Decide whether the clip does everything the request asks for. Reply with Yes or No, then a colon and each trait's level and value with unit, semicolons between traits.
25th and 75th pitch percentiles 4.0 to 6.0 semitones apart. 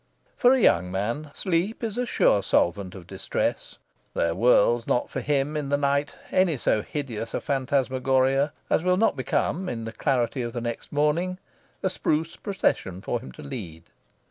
Yes: average, 5.2 semitones